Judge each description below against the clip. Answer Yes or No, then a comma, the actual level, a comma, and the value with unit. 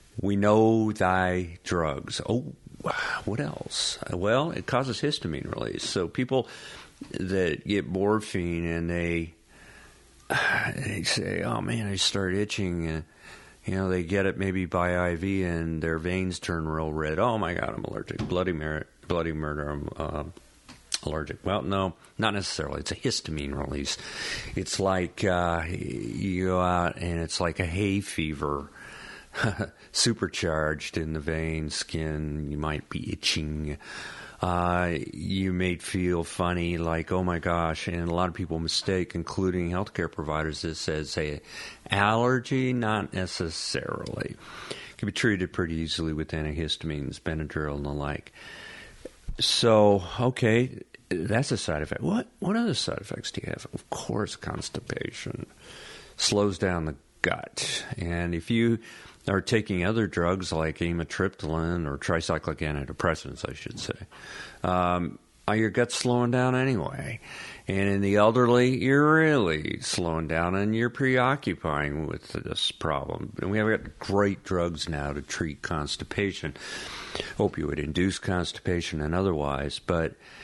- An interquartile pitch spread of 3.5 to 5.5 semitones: Yes, average, 4.0 semitones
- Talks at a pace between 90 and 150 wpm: Yes, average, 145 wpm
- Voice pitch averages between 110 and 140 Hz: No, very low, 90 Hz